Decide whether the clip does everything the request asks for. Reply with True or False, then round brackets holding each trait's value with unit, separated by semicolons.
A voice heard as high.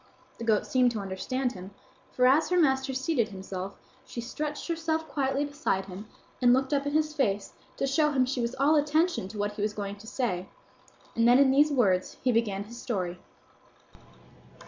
True (250 Hz)